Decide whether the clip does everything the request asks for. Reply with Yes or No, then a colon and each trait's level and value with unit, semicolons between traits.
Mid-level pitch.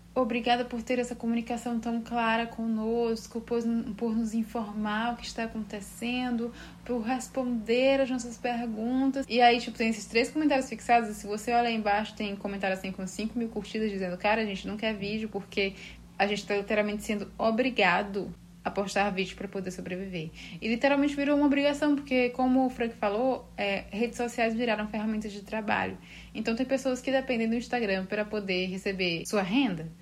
No: high, 225 Hz